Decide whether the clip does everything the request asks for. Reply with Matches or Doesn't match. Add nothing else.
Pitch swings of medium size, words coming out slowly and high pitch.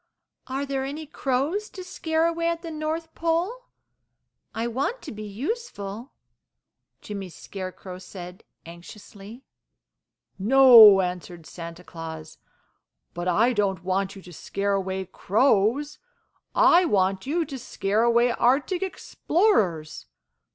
Doesn't match